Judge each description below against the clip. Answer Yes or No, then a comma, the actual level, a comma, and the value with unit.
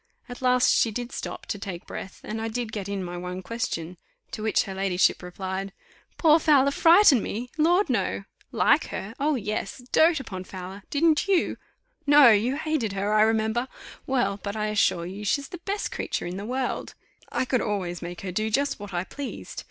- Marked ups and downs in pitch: Yes, wide, 5.7 semitones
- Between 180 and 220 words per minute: Yes, average, 195 wpm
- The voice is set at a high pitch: Yes, high, 220 Hz